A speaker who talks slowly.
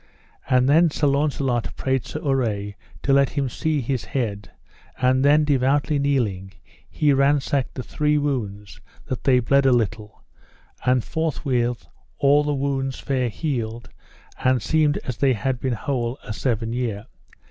No: average, 150 wpm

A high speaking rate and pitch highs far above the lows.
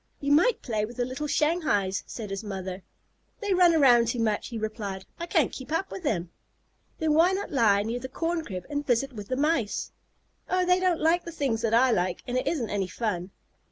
Yes: fast, 220 wpm; wide, 7.3 semitones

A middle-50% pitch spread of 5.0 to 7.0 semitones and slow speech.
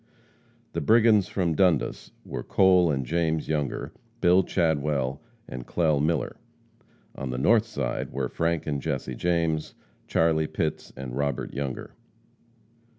No: average, 4.1 semitones; slow, 130 wpm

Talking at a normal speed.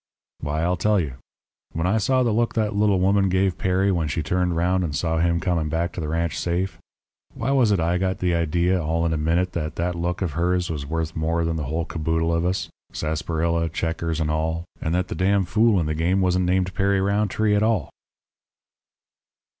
No: fast, 215 wpm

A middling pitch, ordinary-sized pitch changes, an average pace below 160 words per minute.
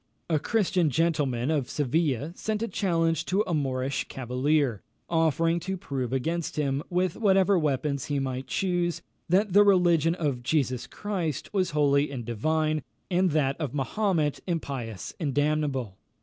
Yes: medium, 155 Hz; average, 4.3 semitones; average, 150 wpm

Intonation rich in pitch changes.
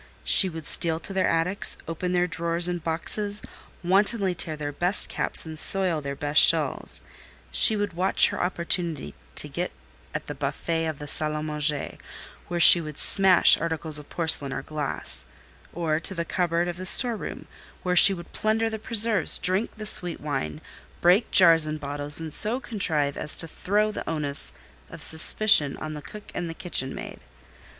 No: average, 3.7 semitones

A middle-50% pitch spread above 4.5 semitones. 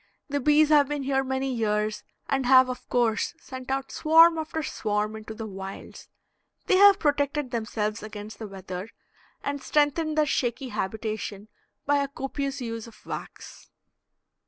Yes: average, 4.9 semitones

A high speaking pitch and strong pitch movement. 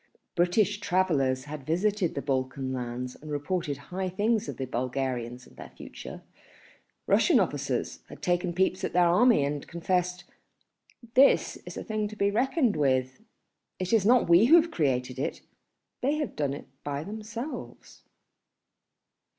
No: medium, 175 Hz; wide, 7.4 semitones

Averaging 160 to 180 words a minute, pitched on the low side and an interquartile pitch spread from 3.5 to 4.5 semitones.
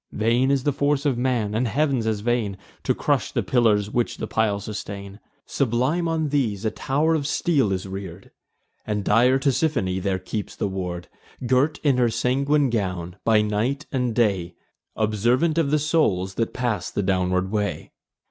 No: average, 170 wpm; low, 115 Hz; average, 5.2 semitones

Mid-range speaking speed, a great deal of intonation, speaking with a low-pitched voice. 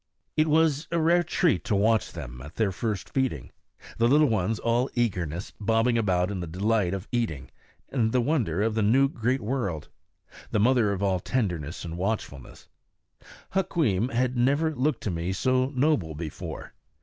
Yes: average, 165 wpm; wide, 6.0 semitones; low, 115 Hz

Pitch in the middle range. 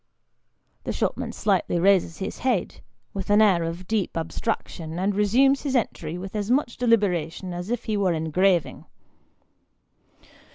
No: high, 195 Hz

